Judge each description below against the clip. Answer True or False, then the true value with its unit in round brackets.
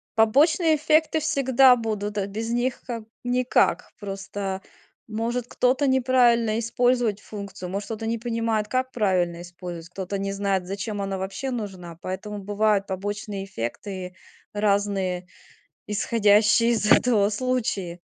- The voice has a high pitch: True (210 Hz)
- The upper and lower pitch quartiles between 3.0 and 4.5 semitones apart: True (3.7 semitones)